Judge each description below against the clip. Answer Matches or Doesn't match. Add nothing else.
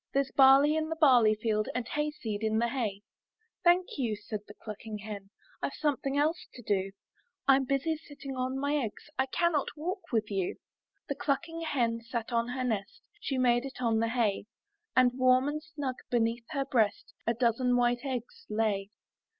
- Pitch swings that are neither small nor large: Matches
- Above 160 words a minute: Matches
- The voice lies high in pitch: Matches